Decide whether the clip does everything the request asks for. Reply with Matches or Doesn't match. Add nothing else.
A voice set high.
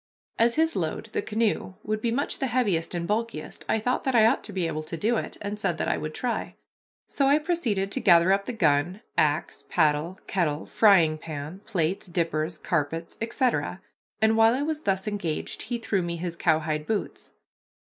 Matches